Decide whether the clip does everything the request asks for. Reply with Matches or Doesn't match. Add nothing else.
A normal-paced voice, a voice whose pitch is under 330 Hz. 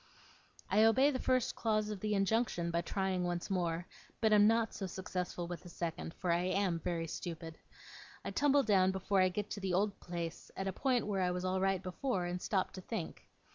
Doesn't match